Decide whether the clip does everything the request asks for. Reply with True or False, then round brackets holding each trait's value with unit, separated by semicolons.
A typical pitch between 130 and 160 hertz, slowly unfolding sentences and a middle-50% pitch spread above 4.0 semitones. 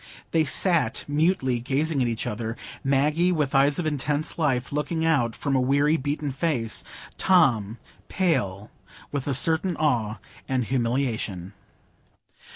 True (140 Hz; 130 wpm; 4.5 semitones)